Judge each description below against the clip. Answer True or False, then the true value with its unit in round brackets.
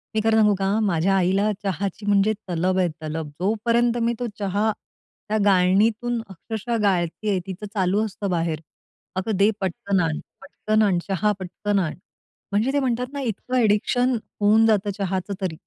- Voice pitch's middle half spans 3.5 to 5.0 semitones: False (2.8 semitones)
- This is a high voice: True (200 Hz)